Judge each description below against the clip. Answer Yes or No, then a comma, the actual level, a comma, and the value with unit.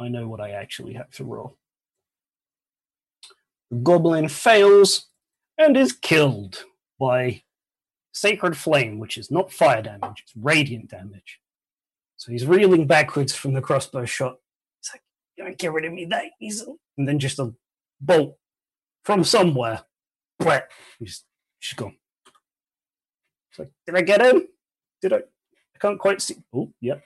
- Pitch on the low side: No, medium, 155 Hz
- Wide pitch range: Yes, wide, 7.7 semitones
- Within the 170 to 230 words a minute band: No, average, 150 wpm